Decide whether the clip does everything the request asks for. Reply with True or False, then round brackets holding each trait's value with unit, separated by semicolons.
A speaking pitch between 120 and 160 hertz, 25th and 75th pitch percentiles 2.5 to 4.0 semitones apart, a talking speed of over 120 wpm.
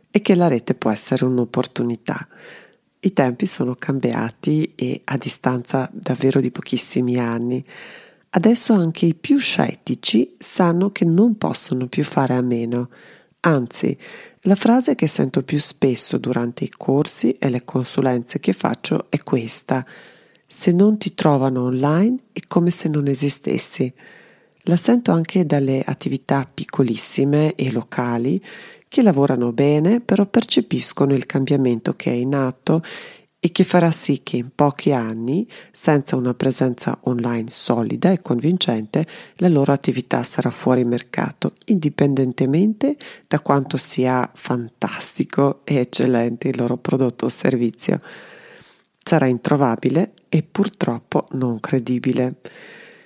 False (140 Hz; 5.5 semitones; 130 wpm)